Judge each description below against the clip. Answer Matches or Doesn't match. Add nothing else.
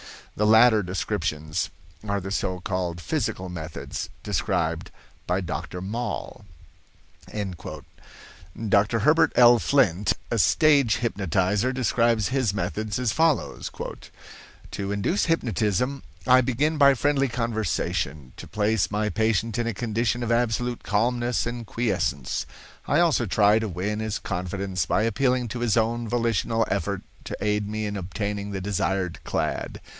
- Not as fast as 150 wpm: Matches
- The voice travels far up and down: Doesn't match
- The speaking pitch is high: Doesn't match